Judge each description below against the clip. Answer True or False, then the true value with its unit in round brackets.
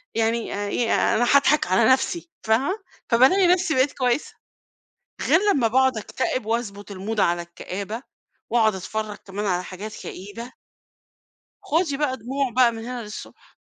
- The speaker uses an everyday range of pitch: True (4.1 semitones)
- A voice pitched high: True (230 Hz)